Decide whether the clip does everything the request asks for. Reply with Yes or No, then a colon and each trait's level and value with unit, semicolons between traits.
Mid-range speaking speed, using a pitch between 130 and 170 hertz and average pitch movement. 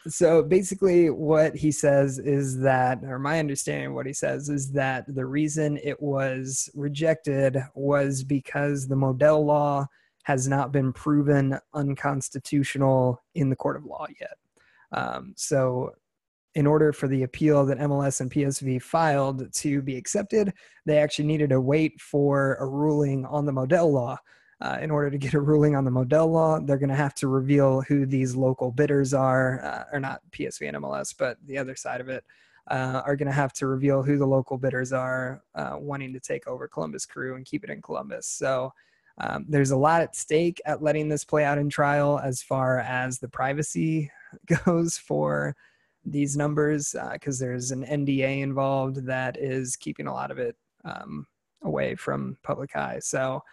No: average, 185 wpm; medium, 140 Hz; narrow, 2.1 semitones